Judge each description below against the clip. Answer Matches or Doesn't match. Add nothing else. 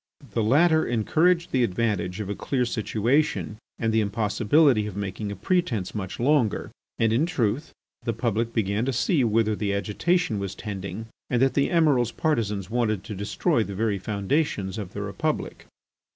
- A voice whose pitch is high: Doesn't match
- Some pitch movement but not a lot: Matches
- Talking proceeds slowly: Doesn't match